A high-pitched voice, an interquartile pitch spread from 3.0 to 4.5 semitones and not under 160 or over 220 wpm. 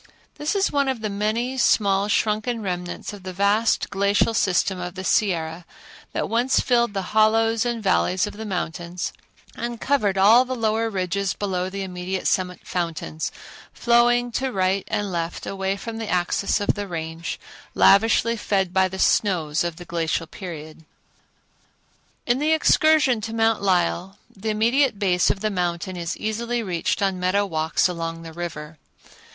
Yes: high, 195 Hz; average, 3.9 semitones; average, 165 wpm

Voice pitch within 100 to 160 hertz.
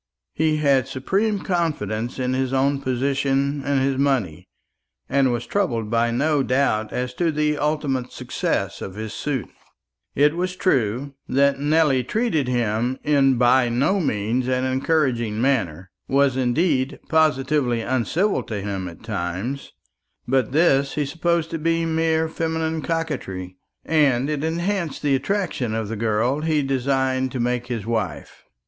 Yes: low, 135 Hz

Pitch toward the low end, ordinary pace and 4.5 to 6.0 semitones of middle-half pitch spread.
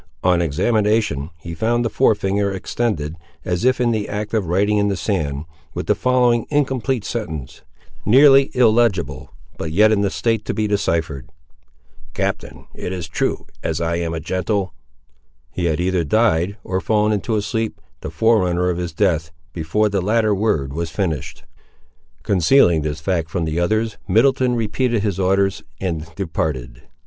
Yes: low, 100 Hz; average, 165 wpm; average, 4.9 semitones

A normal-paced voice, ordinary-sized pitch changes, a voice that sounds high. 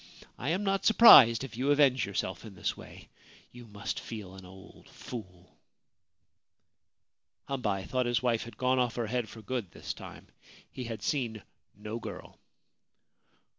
No: average, 165 wpm; average, 3.6 semitones; low, 115 Hz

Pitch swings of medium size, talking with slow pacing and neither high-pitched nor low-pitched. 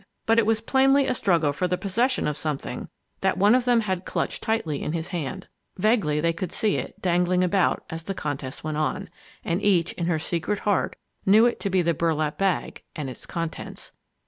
No: average, 4.5 semitones; fast, 205 wpm; medium, 180 Hz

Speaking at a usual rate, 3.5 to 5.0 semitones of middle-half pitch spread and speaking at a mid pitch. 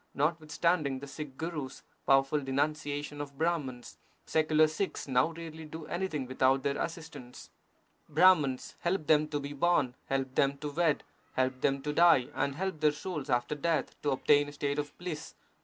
No: average, 165 wpm; average, 2.7 semitones; medium, 150 Hz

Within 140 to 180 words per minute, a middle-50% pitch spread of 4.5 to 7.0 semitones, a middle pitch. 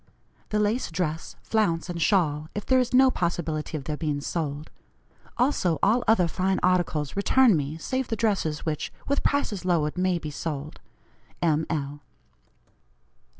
Yes: average, 150 wpm; wide, 5.5 semitones; medium, 170 Hz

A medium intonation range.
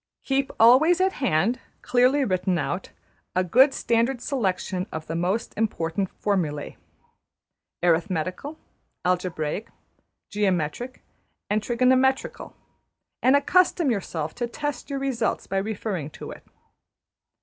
No: wide, 6.4 semitones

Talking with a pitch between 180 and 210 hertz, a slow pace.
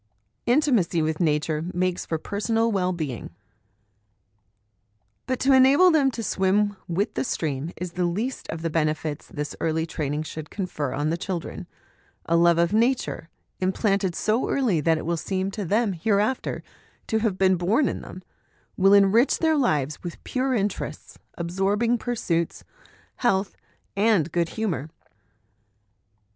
No: high, 190 Hz; average, 150 wpm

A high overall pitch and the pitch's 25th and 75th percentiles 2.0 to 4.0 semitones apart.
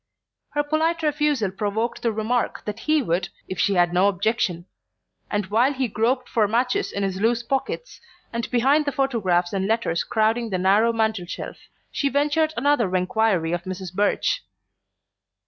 No: high, 220 Hz; wide, 5.6 semitones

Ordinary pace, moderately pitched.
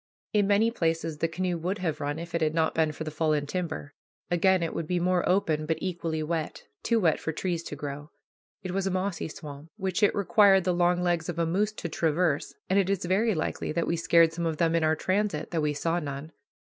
No: fast, 240 wpm; medium, 170 Hz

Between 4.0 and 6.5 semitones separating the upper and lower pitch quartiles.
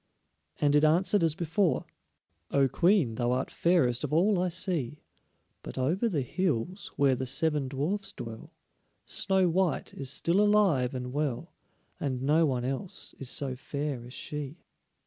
Yes: wide, 5.6 semitones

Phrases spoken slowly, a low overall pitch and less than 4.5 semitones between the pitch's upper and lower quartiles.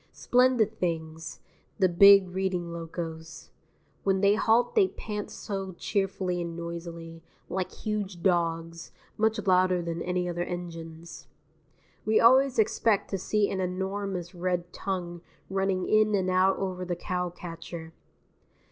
No: slow, 130 wpm; medium, 185 Hz; narrow, 2.6 semitones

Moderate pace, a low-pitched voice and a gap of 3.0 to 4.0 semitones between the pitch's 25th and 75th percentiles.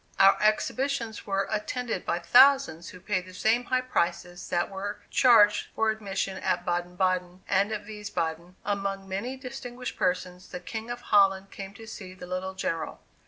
No: average, 165 wpm; high, 195 Hz; average, 3.3 semitones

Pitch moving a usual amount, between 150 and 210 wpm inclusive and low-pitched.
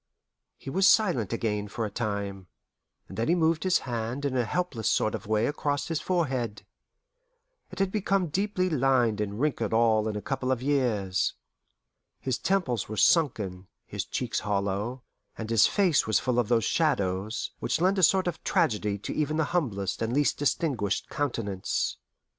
No: wide, 6.9 semitones; average, 170 wpm; low, 120 Hz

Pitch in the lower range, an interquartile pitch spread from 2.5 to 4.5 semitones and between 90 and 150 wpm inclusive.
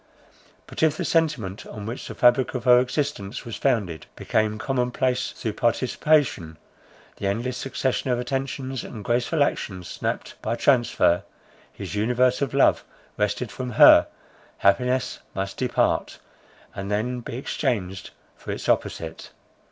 Yes: low, 125 Hz; average, 3.9 semitones; average, 140 wpm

